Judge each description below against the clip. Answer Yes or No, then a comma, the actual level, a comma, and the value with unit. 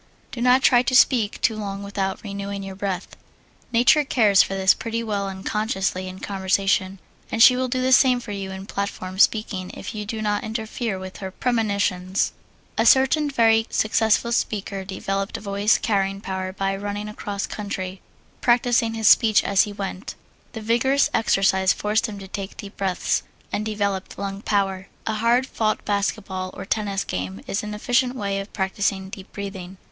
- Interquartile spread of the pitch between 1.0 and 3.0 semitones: Yes, narrow, 2.6 semitones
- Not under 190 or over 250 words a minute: No, average, 170 wpm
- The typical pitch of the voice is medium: No, high, 200 Hz